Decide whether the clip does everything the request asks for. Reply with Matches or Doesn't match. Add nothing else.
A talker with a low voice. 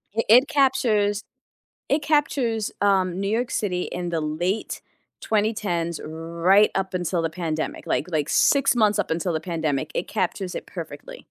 Doesn't match